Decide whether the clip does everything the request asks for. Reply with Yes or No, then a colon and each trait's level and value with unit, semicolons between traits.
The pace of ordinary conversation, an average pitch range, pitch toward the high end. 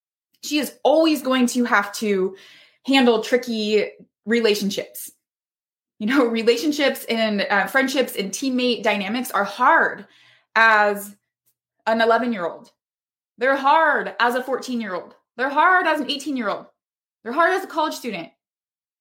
Yes: average, 145 wpm; average, 4.4 semitones; high, 235 Hz